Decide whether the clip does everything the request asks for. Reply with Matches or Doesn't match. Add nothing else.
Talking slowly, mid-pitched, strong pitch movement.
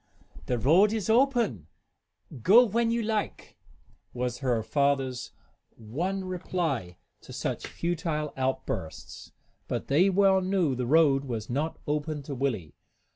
Matches